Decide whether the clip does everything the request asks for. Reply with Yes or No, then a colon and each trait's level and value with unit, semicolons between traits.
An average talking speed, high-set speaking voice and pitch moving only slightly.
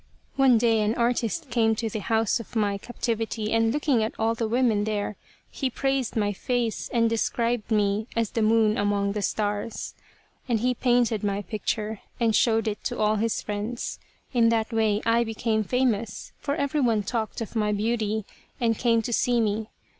Yes: average, 180 wpm; high, 225 Hz; narrow, 1.8 semitones